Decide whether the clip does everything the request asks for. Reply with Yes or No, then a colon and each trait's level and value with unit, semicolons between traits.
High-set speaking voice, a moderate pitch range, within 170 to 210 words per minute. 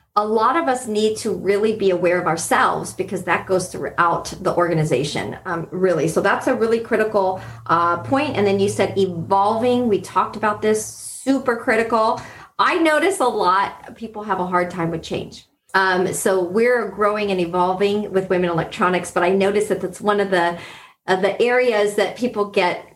Yes: high, 195 Hz; average, 3.3 semitones; average, 185 wpm